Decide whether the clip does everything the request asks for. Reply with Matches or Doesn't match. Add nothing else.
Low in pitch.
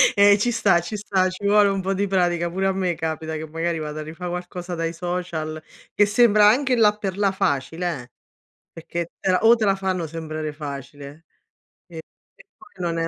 Doesn't match